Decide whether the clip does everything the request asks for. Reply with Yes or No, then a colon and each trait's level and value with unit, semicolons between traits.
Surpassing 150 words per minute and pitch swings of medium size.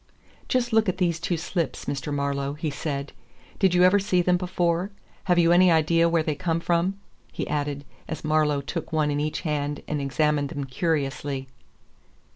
Yes: average, 180 wpm; average, 3.4 semitones